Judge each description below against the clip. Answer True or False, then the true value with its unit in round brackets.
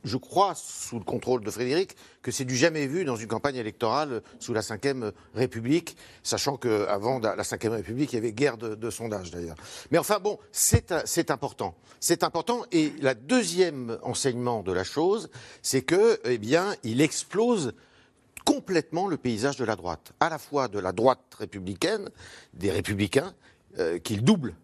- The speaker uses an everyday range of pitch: False (6.7 semitones)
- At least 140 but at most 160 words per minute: False (180 wpm)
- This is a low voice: True (125 Hz)